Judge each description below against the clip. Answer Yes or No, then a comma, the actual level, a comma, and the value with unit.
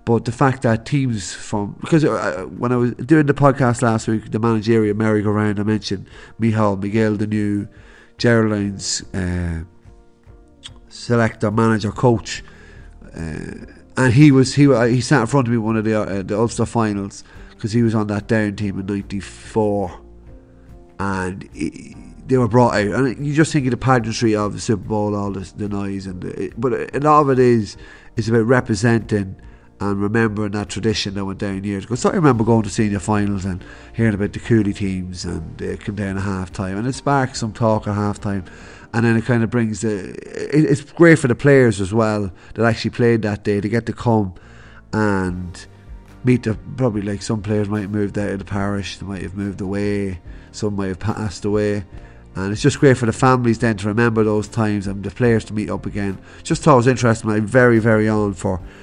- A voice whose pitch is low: Yes, low, 110 Hz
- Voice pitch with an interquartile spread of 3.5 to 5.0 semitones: No, average, 2.7 semitones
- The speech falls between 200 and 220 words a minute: Yes, fast, 205 wpm